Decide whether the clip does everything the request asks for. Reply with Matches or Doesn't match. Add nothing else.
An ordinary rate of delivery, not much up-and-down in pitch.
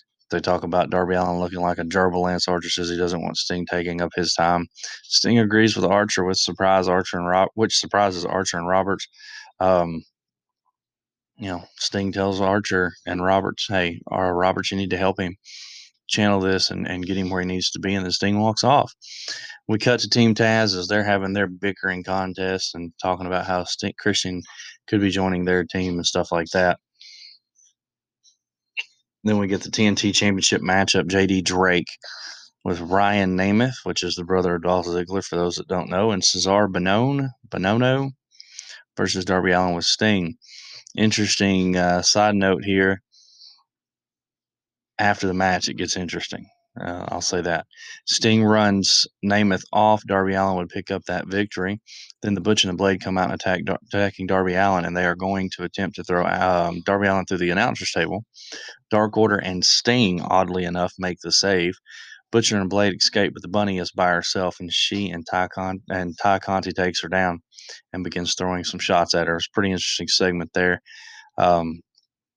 Matches